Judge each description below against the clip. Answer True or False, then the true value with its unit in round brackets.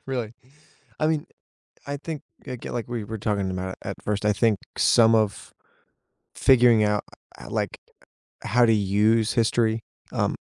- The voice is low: True (110 Hz)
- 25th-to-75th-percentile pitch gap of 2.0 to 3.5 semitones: True (2.6 semitones)